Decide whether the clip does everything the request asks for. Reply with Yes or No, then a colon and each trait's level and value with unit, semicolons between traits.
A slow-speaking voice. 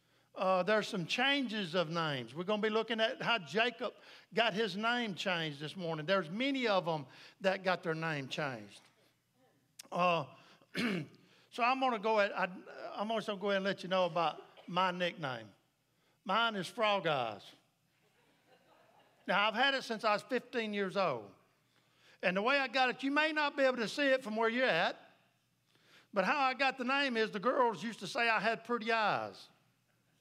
No: average, 195 wpm